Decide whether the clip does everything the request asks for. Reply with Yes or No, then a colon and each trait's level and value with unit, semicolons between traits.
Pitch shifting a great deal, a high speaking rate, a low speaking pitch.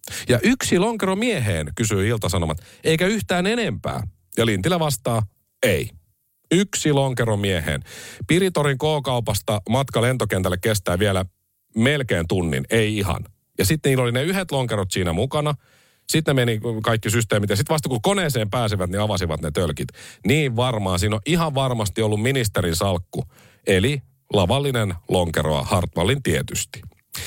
No: wide, 6.3 semitones; average, 140 wpm; low, 115 Hz